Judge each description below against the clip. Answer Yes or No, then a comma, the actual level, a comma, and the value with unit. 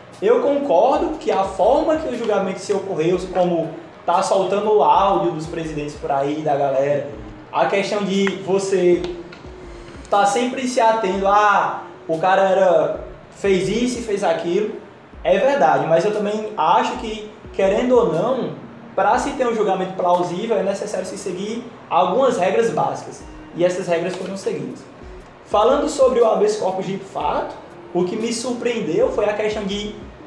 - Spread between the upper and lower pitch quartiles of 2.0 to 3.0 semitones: No, average, 3.9 semitones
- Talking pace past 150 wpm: Yes, average, 160 wpm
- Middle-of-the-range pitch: No, high, 195 Hz